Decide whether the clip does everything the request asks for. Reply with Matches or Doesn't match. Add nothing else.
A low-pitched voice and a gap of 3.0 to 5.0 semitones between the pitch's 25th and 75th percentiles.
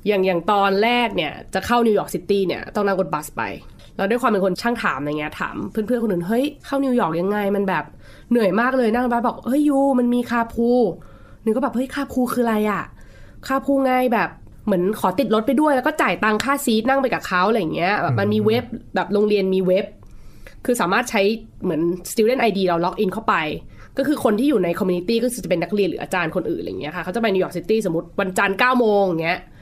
Doesn't match